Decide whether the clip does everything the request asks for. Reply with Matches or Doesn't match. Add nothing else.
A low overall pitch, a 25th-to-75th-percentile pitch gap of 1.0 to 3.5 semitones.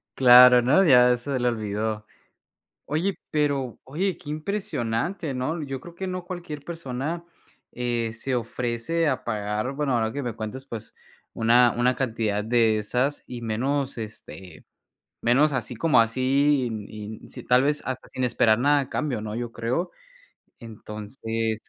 Doesn't match